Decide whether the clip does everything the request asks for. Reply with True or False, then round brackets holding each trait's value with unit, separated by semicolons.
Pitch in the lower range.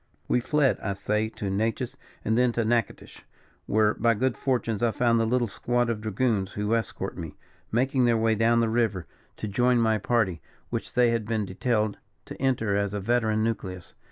True (115 Hz)